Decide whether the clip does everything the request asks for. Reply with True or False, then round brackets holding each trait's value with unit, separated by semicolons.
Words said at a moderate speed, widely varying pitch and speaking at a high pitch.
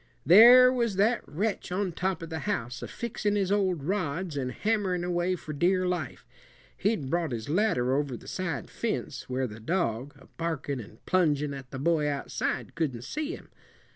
False (180 wpm; 5.7 semitones; 170 Hz)